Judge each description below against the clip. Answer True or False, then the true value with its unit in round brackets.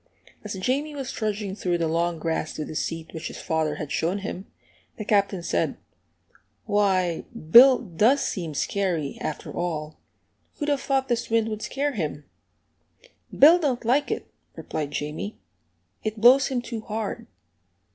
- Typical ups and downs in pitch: False (6.7 semitones)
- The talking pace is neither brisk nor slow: True (155 wpm)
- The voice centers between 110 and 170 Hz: False (205 Hz)